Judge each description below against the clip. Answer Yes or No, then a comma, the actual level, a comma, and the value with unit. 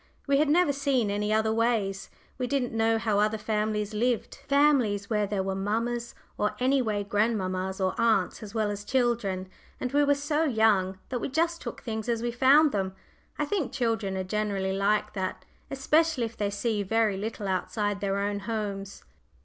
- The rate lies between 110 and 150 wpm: No, average, 185 wpm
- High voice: Yes, high, 220 Hz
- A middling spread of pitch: Yes, average, 3.6 semitones